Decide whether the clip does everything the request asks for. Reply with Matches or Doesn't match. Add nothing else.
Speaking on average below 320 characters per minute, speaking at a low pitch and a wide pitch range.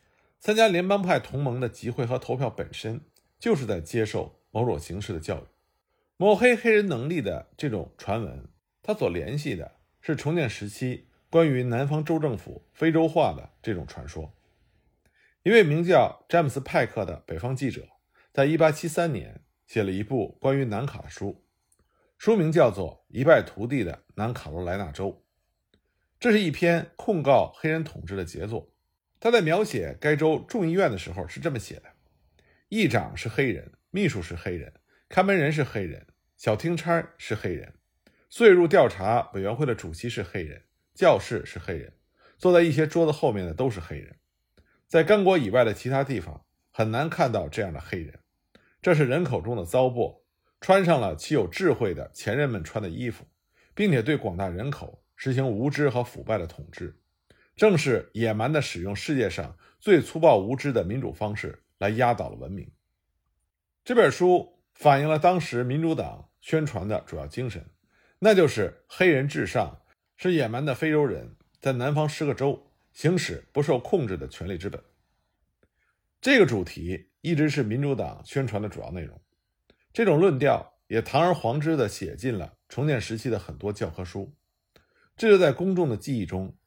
Matches